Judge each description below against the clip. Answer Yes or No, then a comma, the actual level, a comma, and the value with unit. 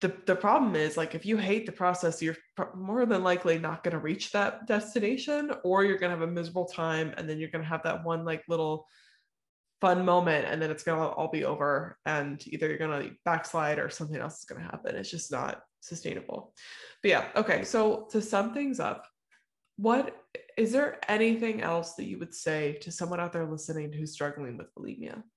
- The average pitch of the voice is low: No, medium, 170 Hz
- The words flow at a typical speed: No, fast, 215 wpm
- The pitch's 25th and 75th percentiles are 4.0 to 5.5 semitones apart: Yes, average, 4.9 semitones